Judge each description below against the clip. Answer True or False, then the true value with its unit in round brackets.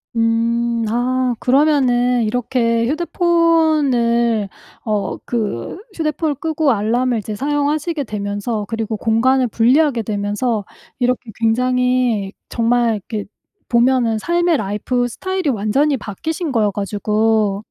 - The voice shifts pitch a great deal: False (4.0 semitones)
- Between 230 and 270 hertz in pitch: True (240 Hz)